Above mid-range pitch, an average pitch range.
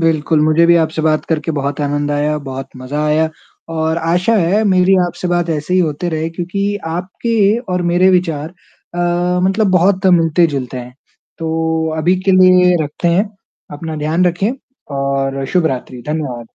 No: medium, 165 Hz; average, 3.3 semitones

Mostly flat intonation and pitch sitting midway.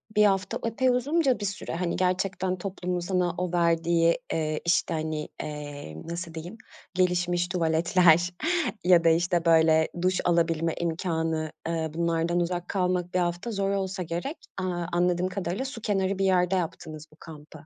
Yes: narrow, 2.1 semitones; medium, 175 Hz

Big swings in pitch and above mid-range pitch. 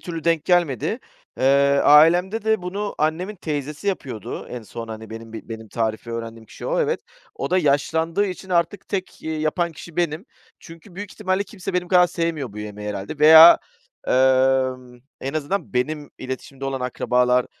No: wide, 6.0 semitones; medium, 155 Hz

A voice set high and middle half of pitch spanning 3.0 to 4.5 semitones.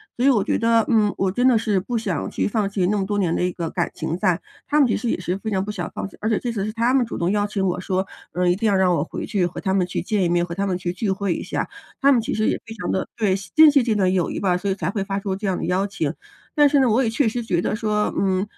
Yes: high, 200 Hz; average, 3.5 semitones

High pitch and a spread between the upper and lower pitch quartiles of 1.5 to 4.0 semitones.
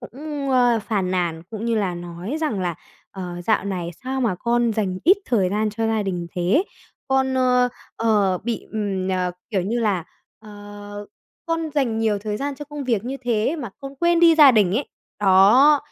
No: high, 220 Hz; average, 5.3 semitones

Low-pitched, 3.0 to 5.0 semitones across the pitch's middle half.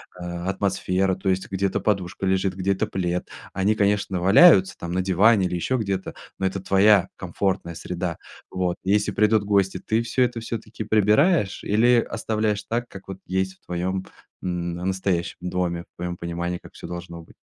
No: very low, 95 Hz; narrow, 2.6 semitones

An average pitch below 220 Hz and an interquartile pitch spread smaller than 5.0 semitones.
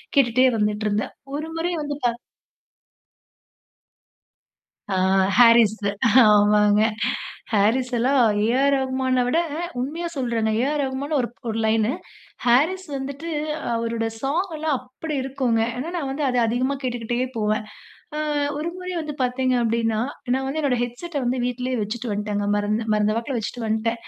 No: very high, 250 Hz; average, 3.7 semitones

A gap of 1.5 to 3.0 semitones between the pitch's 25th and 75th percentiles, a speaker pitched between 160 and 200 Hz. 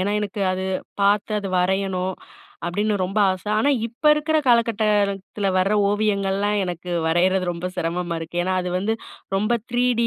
Yes: narrow, 2.5 semitones; high, 195 Hz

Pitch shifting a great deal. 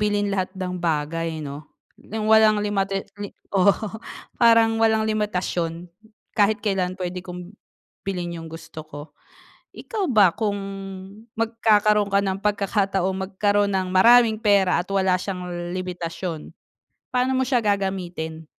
No: average, 3.0 semitones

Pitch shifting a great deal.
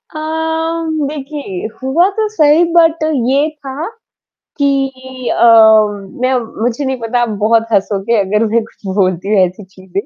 Yes: wide, 6.5 semitones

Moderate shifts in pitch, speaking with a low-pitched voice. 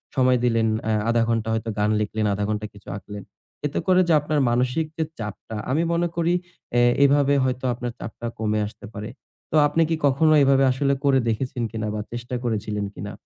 Yes: average, 4.5 semitones; low, 120 Hz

